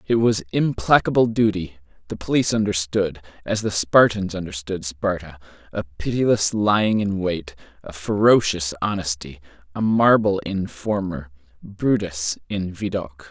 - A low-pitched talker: Yes, very low, 95 Hz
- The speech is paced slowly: Yes, slow, 115 wpm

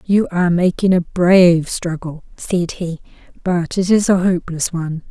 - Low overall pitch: No, medium, 175 Hz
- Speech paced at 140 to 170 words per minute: Yes, average, 165 wpm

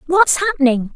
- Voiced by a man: No, female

